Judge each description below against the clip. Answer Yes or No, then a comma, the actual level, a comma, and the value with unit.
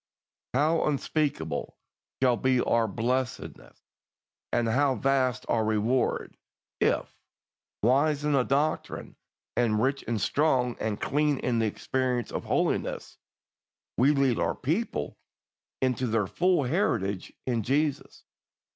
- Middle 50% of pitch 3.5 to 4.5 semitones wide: Yes, average, 3.8 semitones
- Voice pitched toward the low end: Yes, low, 130 Hz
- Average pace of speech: No, slow, 120 wpm